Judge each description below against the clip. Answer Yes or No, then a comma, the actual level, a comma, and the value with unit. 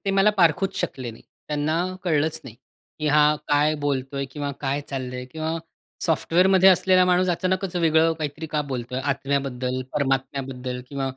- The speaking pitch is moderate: Yes, medium, 145 Hz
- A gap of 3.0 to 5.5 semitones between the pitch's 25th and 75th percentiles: Yes, average, 3.7 semitones